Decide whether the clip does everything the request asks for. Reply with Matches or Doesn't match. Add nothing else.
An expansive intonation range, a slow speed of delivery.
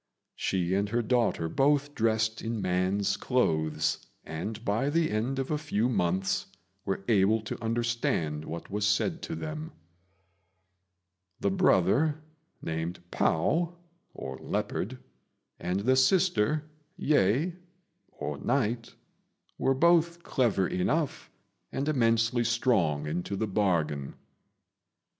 Matches